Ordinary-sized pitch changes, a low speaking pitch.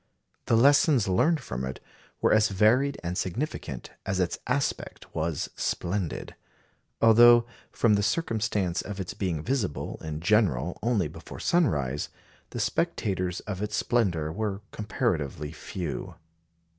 No: wide, 5.7 semitones; low, 100 Hz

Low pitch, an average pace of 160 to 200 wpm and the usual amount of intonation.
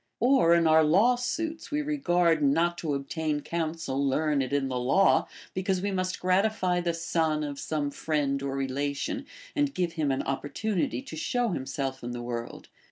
No: medium, 160 Hz; average, 170 wpm; average, 5.0 semitones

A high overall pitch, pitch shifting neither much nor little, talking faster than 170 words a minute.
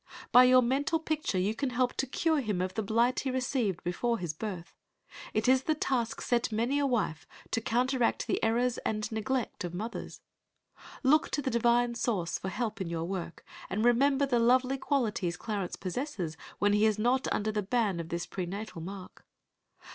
Yes: high, 230 Hz; average, 4.6 semitones; average, 185 wpm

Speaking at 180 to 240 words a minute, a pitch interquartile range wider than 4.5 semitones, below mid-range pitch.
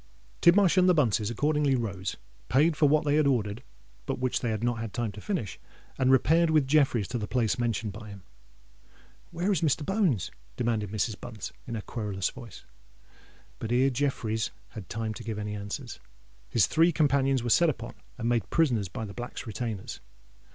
Yes: average, 185 wpm; average, 5.3 semitones; low, 120 Hz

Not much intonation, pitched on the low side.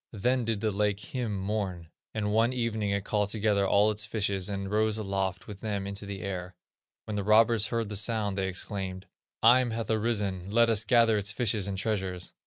Yes: narrow, 2.1 semitones; low, 105 Hz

